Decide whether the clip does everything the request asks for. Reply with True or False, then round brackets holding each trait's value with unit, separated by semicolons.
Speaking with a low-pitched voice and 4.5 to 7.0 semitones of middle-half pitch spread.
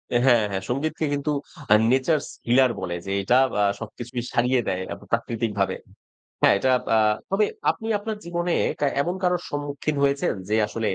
True (130 Hz; 5.2 semitones)